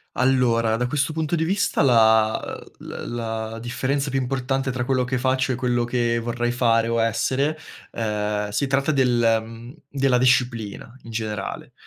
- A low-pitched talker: Yes, low, 125 Hz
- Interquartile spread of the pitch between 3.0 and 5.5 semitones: No, narrow, 2.6 semitones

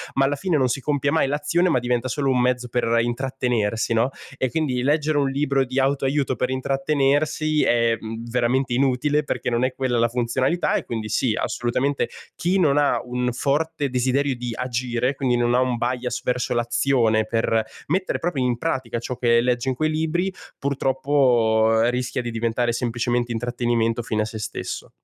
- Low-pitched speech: Yes, low, 125 Hz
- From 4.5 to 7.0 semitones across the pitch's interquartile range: No, average, 2.7 semitones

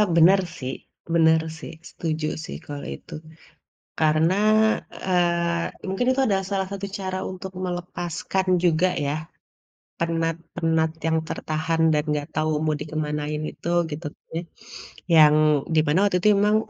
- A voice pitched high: No, medium, 165 Hz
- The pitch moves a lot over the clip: No, average, 2.9 semitones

